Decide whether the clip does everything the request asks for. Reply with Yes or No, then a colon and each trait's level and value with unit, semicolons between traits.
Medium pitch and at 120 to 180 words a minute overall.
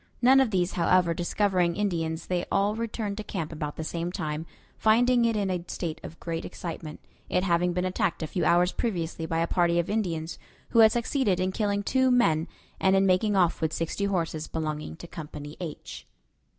No: medium, 180 Hz; average, 195 wpm